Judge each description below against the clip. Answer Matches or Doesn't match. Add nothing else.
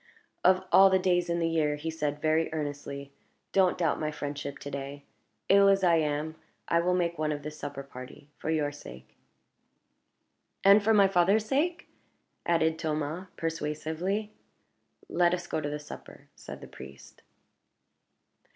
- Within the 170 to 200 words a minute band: Doesn't match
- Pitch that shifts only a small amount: Doesn't match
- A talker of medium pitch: Matches